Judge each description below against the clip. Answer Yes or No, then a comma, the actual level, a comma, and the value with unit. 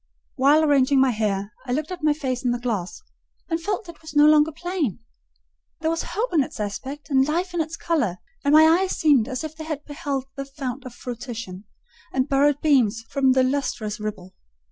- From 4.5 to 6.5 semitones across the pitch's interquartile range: No, average, 4.1 semitones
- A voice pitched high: Yes, very high, 280 Hz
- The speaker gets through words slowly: No, fast, 205 wpm